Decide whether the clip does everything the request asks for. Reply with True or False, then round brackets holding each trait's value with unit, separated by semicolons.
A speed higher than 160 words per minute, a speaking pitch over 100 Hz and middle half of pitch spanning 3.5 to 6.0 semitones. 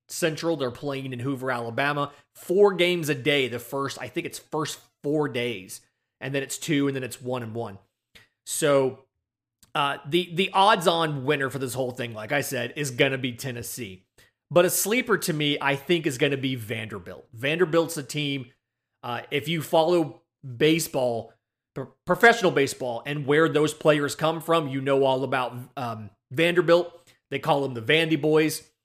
True (185 wpm; 140 Hz; 4.2 semitones)